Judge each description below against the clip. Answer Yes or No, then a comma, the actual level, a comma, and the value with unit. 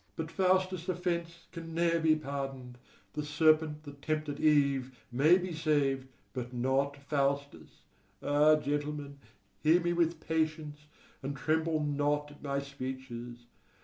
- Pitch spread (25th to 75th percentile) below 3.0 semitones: Yes, narrow, 2.5 semitones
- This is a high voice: No, medium, 150 Hz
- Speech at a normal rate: No, slow, 130 wpm